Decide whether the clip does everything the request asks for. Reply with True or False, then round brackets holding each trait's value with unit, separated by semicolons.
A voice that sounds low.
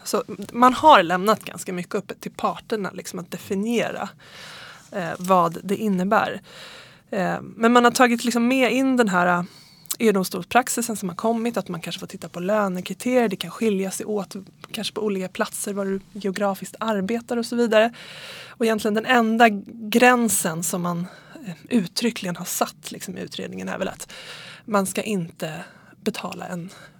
False (205 Hz)